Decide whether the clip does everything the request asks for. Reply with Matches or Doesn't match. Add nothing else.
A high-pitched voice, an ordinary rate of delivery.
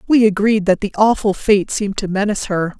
Doesn't match